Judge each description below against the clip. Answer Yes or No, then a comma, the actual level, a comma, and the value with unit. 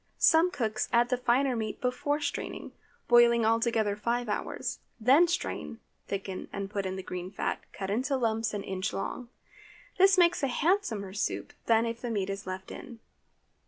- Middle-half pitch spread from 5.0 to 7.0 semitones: No, average, 3.9 semitones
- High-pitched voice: Yes, high, 230 Hz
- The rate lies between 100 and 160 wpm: No, average, 175 wpm